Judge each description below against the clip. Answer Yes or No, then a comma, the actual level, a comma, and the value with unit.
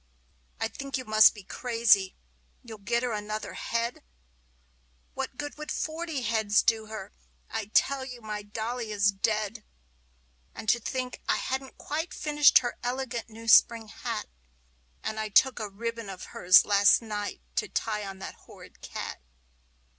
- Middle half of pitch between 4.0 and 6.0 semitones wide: No, average, 3.1 semitones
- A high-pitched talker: Yes, high, 225 Hz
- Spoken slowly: No, average, 160 wpm